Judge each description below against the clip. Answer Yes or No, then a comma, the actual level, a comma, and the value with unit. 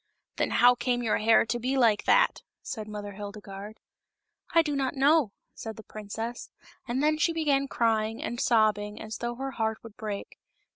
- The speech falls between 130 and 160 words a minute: No, average, 195 wpm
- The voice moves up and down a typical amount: Yes, average, 3.8 semitones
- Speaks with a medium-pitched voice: No, high, 230 Hz